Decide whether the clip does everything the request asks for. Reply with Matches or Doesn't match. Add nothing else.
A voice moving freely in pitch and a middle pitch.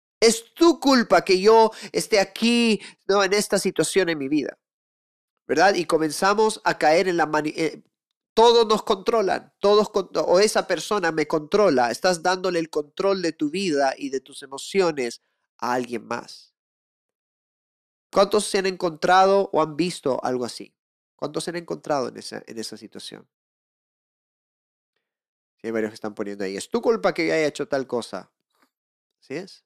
Matches